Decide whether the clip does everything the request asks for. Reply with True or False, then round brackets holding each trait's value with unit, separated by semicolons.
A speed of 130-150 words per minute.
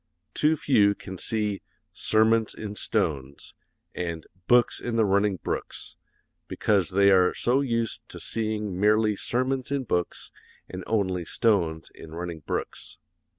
True (135 wpm)